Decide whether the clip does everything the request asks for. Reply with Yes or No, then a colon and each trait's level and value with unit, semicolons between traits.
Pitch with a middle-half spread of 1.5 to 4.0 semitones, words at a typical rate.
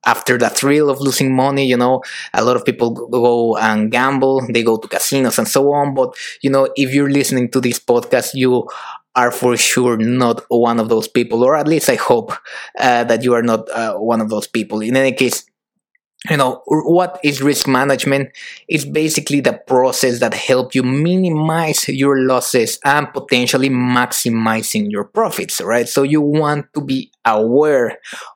Yes: average, 2.9 semitones; average, 180 wpm